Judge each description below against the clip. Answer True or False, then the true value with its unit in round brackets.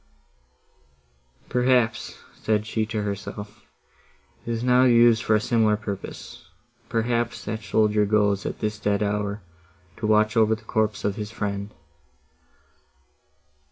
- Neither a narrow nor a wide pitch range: False (1.5 semitones)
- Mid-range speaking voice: False (110 Hz)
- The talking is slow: True (125 wpm)